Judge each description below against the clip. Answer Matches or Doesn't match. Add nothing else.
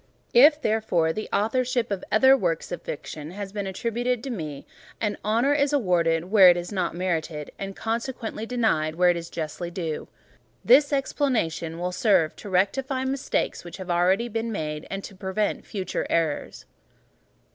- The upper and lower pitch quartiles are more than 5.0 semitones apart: Matches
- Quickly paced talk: Doesn't match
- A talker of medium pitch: Doesn't match